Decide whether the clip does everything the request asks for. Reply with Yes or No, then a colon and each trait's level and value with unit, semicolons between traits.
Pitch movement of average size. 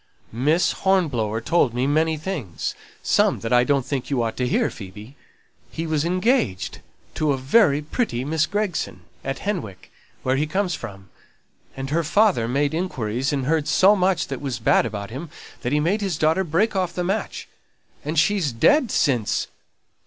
No: wide, 6.6 semitones